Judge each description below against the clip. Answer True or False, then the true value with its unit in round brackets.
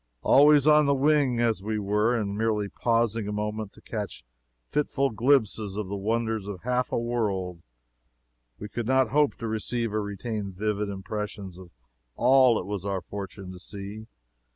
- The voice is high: False (110 Hz)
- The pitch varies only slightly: False (3.0 semitones)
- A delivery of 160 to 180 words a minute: True (170 wpm)